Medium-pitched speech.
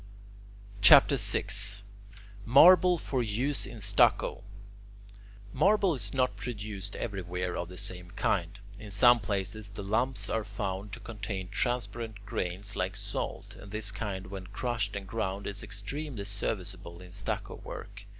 No: low, 100 Hz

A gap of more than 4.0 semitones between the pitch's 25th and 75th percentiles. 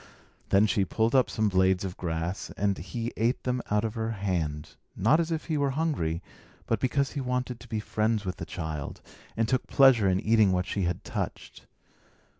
Yes: average, 5.1 semitones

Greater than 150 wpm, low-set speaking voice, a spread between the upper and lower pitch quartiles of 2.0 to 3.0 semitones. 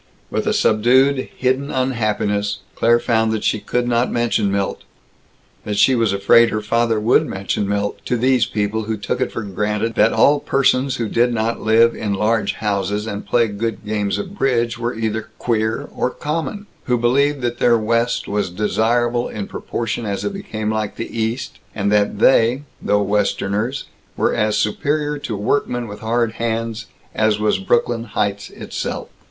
Yes: average, 170 wpm; low, 115 Hz; narrow, 2.5 semitones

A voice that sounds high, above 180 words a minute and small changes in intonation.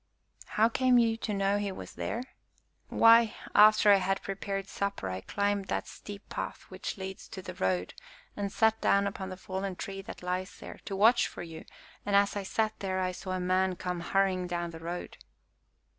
Yes: high, 195 Hz; average, 195 wpm; narrow, 1.9 semitones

